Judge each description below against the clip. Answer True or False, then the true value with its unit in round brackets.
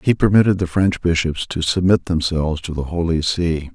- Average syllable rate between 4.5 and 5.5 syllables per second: True (5.2 syllables/s)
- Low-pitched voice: True (85 Hz)